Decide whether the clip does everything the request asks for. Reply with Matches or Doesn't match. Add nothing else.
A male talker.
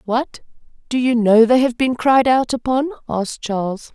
Doesn't match